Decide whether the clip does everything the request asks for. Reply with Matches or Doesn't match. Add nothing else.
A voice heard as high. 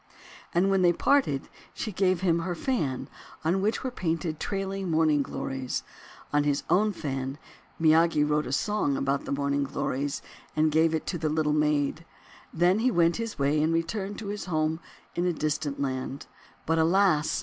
Doesn't match